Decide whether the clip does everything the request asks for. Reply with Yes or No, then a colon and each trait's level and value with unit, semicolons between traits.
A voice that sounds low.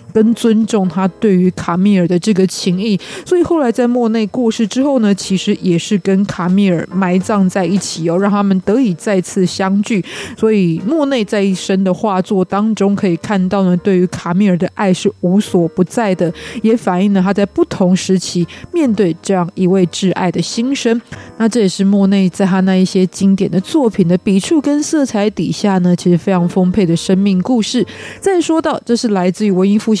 No: high, 195 Hz